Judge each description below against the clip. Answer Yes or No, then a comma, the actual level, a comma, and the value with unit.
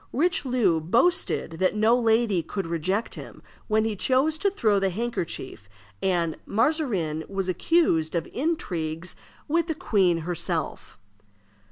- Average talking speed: No, slow, 130 wpm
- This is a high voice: Yes, high, 200 Hz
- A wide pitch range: Yes, wide, 6.8 semitones